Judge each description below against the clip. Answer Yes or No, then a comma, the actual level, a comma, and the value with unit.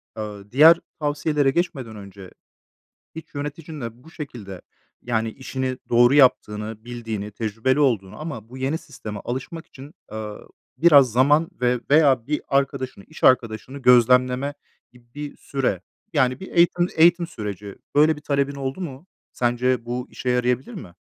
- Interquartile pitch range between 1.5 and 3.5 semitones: No, average, 4.3 semitones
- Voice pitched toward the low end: Yes, low, 130 Hz